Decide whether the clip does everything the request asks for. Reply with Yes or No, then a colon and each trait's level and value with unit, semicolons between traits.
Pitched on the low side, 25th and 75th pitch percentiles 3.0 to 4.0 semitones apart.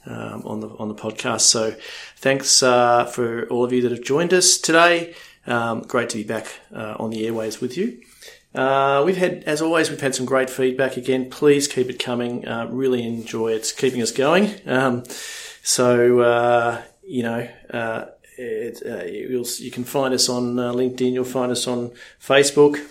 No: low, 125 Hz; narrow, 2.4 semitones